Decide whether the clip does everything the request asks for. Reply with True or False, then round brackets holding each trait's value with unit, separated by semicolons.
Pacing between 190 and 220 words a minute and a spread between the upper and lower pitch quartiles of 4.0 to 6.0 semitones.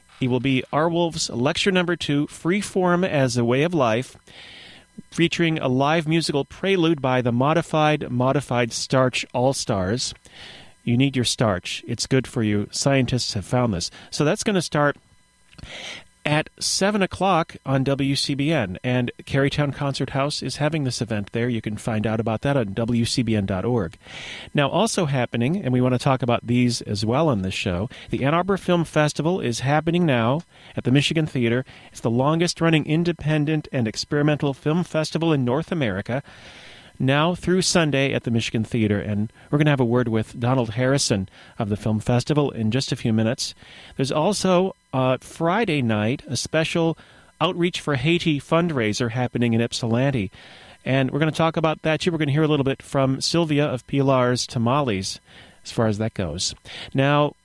False (180 wpm; 4.7 semitones)